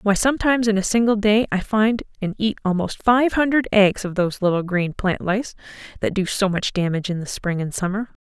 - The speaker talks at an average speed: No, fast, 220 wpm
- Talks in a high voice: Yes, high, 205 Hz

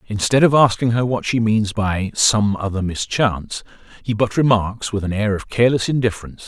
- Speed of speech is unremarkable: Yes, average, 185 wpm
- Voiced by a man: Yes, male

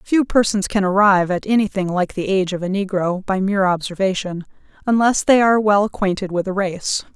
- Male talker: No, female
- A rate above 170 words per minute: Yes, average, 195 wpm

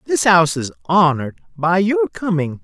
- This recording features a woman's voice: No, male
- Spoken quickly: No, average, 160 wpm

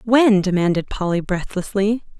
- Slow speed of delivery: Yes, slow, 110 wpm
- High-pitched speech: Yes, high, 200 Hz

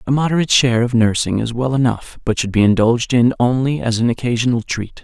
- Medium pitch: No, low, 120 Hz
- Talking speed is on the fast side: Yes, fast, 215 wpm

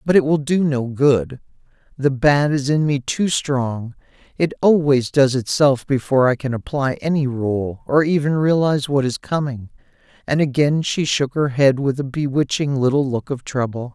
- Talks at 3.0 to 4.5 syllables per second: No, 4.7 syllables/s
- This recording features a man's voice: Yes, male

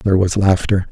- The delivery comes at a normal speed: Yes, average, 195 wpm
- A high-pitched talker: No, very low, 95 Hz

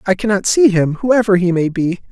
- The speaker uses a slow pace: No, fast, 225 wpm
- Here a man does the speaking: Yes, male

